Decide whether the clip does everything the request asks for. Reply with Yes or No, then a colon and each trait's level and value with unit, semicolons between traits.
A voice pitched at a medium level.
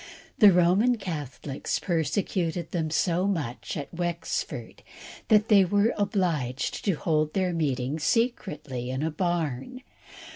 Yes: medium, 170 Hz